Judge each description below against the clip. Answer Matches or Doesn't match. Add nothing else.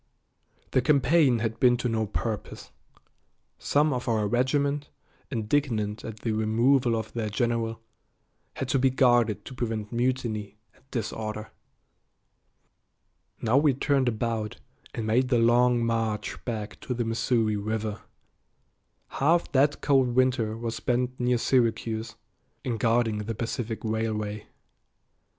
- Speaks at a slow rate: Matches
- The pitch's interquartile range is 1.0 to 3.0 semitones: Matches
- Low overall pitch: Matches